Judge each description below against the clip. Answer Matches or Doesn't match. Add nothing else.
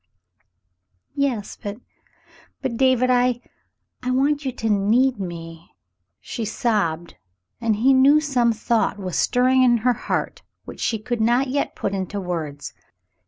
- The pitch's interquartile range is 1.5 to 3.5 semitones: Doesn't match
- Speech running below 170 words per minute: Matches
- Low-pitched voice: Doesn't match